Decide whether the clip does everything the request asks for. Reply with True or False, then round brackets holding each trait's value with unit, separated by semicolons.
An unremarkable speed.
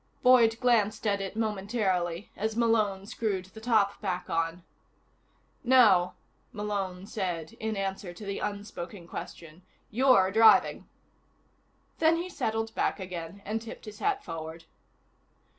False (125 wpm)